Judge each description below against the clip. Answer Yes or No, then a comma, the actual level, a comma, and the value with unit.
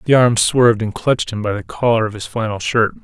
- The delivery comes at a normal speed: No, fast, 255 wpm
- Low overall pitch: Yes, low, 115 Hz